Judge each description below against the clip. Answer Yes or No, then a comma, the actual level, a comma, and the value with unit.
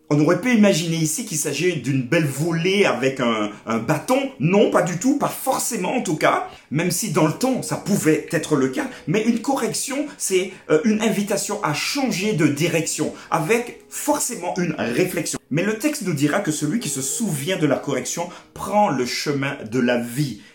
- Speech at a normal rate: Yes, average, 195 wpm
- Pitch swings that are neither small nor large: No, wide, 6.2 semitones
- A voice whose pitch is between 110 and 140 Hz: No, medium, 170 Hz